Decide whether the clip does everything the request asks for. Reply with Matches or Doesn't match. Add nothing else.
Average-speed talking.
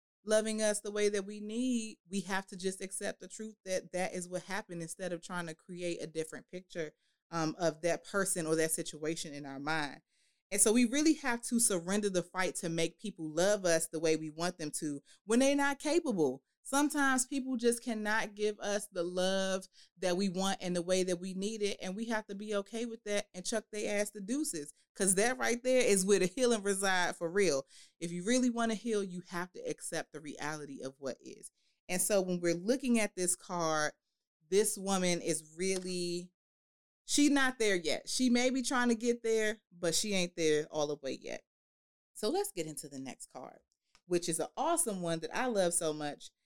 Doesn't match